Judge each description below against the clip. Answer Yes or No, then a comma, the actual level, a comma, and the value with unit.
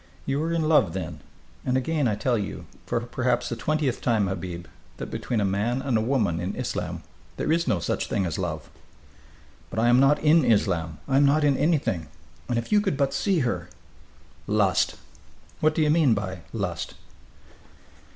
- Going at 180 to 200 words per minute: Yes, average, 190 wpm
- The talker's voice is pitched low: Yes, low, 120 Hz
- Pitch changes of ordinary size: No, wide, 7.2 semitones